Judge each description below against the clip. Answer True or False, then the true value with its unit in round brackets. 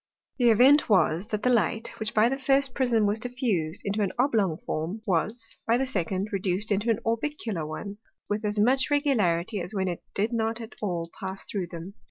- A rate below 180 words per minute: False (200 wpm)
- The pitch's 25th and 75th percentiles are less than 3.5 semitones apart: False (4.0 semitones)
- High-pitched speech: True (215 Hz)